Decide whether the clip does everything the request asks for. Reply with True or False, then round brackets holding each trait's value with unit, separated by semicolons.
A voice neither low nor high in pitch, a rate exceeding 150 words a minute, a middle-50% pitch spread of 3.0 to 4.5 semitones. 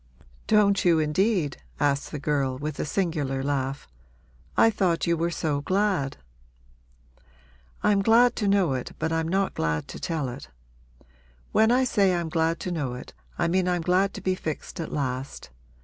False (165 Hz; 170 wpm; 5.2 semitones)